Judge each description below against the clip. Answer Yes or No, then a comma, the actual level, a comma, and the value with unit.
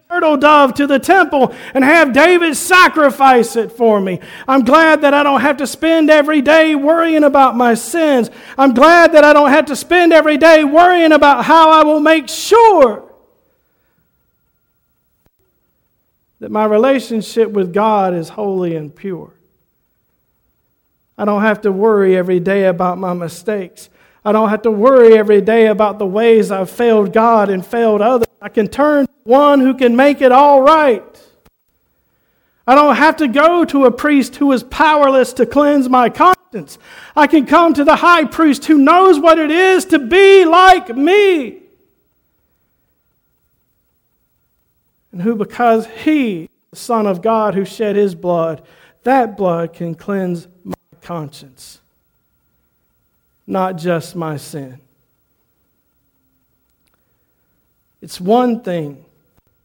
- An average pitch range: No, wide, 7.3 semitones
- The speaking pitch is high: Yes, very high, 250 Hz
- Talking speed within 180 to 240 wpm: No, average, 145 wpm